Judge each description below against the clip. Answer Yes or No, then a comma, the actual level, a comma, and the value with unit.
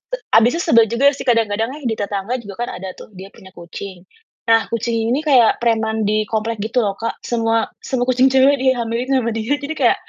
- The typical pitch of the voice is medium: No, high, 230 Hz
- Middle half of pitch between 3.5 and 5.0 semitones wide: No, average, 2.9 semitones